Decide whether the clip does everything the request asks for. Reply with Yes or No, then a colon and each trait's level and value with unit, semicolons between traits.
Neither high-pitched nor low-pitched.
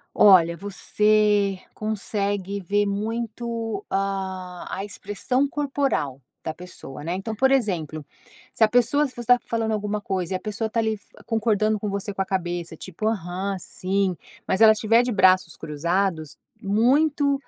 No: high, 205 Hz